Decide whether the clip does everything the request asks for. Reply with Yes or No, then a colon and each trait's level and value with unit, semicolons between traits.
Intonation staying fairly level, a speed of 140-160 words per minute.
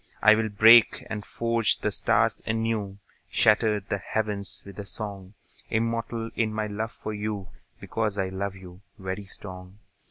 Yes: narrow, 2.1 semitones; average, 150 wpm